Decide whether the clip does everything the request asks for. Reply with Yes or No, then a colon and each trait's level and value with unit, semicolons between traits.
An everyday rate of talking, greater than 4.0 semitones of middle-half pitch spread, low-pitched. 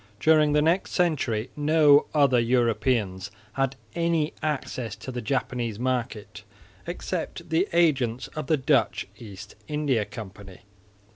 No: slow, 125 wpm; average, 5.0 semitones; low, 130 Hz